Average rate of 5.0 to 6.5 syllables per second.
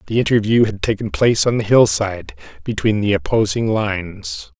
Yes: 5.4 syllables/s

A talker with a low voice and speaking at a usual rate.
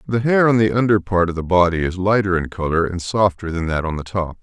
No: very low, 95 Hz; fast, 270 wpm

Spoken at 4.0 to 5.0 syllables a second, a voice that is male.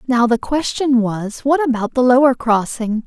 No: 4.5 syllables/s; female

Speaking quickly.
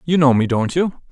Yes: fast, 270 wpm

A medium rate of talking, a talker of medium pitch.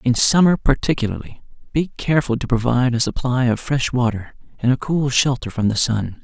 No: average, 185 wpm; low, 125 Hz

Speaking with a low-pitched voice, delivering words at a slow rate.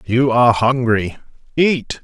Yes: low, 125 Hz; slow, 120 wpm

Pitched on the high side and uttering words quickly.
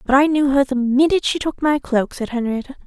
Yes: very high, 270 Hz; fast, 250 wpm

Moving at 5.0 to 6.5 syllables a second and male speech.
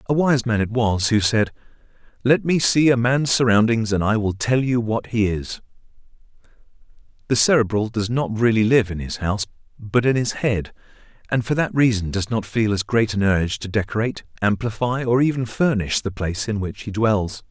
Yes: 5.2 syllables/s; male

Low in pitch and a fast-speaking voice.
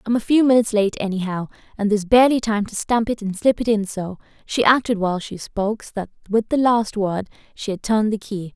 No: high, 215 Hz; fast, 240 wpm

